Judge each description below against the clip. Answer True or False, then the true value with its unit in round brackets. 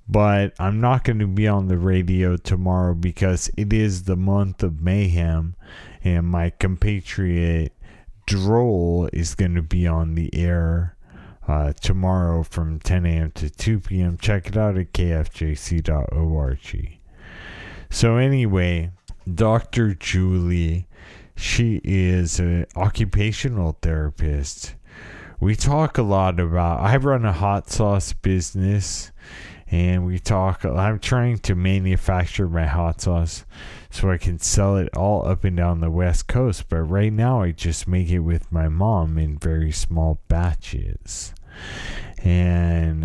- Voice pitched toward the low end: True (90 Hz)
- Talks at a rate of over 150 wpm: False (135 wpm)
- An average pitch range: True (3.1 semitones)